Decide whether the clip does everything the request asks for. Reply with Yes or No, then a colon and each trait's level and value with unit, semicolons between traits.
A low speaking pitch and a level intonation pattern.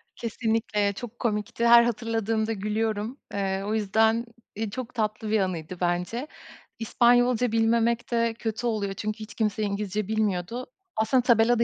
No: high, 220 Hz; narrow, 2.0 semitones